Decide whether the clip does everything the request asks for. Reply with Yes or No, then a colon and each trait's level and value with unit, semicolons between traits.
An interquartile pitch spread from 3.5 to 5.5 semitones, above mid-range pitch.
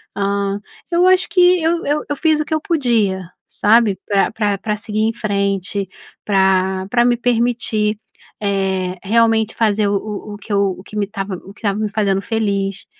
No: average, 2.9 semitones; high, 210 Hz